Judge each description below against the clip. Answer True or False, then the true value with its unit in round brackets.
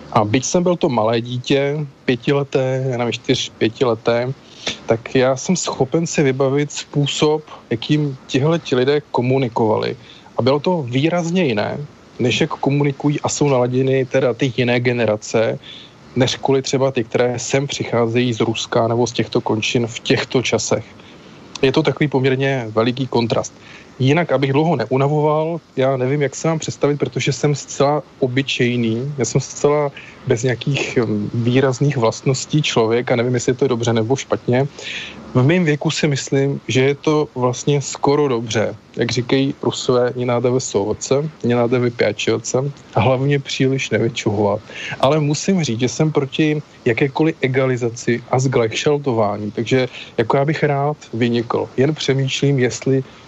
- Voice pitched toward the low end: True (130 Hz)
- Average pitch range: True (3.1 semitones)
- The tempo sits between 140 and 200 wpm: True (150 wpm)